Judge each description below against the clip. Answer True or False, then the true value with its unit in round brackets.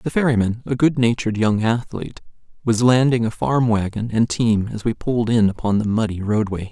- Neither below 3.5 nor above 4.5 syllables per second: False (5.5 syllables/s)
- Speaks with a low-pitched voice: True (115 Hz)